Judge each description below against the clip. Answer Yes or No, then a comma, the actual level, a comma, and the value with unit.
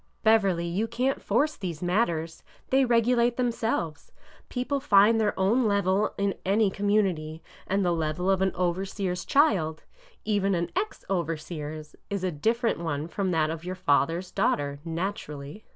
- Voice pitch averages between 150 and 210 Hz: Yes, high, 190 Hz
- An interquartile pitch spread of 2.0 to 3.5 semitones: No, average, 4.9 semitones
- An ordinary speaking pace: Yes, average, 170 wpm